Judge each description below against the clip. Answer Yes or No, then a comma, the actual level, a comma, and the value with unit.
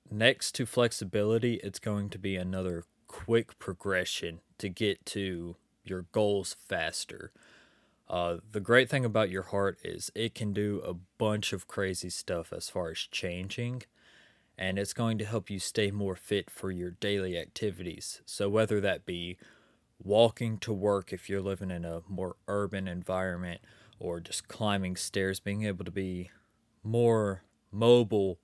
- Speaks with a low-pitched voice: Yes, low, 100 Hz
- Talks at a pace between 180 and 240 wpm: No, average, 155 wpm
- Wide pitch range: No, average, 2.7 semitones